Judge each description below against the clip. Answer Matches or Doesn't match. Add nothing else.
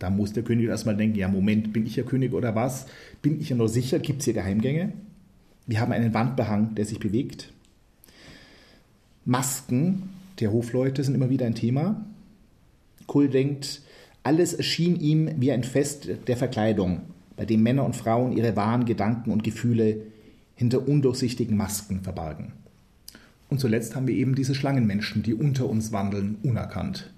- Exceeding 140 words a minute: Matches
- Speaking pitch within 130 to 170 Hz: Doesn't match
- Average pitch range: Matches